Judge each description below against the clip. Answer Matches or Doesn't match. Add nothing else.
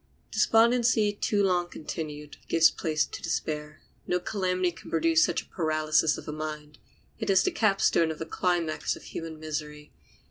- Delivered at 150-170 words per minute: Matches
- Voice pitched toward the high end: Doesn't match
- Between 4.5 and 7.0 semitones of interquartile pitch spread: Doesn't match